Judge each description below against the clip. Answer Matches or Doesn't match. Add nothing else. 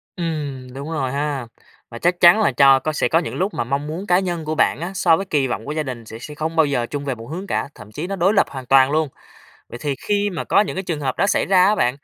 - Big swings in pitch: Doesn't match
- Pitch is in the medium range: Matches